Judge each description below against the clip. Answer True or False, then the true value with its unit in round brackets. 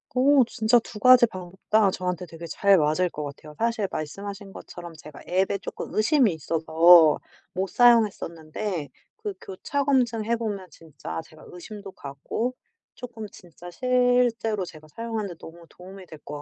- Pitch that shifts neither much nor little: False (5.7 semitones)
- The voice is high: True (195 Hz)